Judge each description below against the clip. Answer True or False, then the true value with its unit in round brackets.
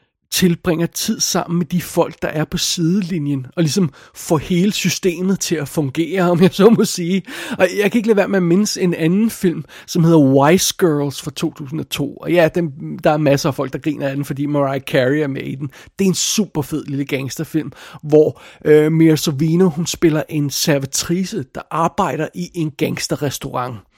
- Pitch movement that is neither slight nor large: True (3.4 semitones)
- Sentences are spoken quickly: False (200 wpm)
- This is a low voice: False (165 Hz)